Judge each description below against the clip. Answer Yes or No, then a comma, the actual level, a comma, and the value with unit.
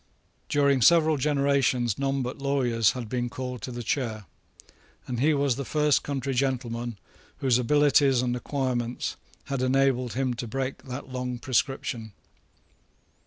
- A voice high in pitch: No, low, 130 Hz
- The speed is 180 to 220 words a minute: No, average, 140 wpm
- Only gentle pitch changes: Yes, narrow, 2.2 semitones